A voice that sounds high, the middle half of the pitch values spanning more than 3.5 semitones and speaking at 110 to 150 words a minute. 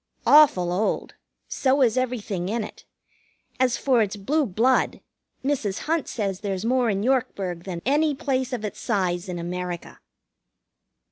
Yes: high, 220 Hz; wide, 5.6 semitones; average, 145 wpm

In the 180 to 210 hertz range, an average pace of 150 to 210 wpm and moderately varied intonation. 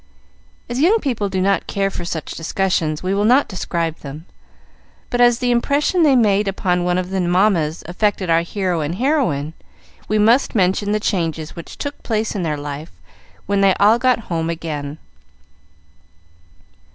Yes: high, 190 Hz; average, 165 wpm; average, 5.0 semitones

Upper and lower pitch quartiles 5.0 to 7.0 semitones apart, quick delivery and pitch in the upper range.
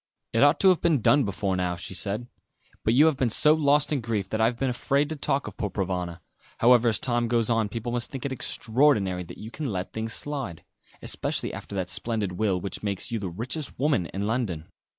No: wide, 5.4 semitones; fast, 230 wpm; low, 115 Hz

